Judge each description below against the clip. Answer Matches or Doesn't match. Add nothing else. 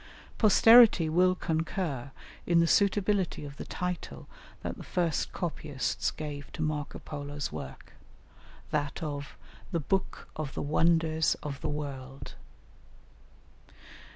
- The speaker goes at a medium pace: Doesn't match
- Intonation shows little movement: Doesn't match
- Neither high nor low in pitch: Matches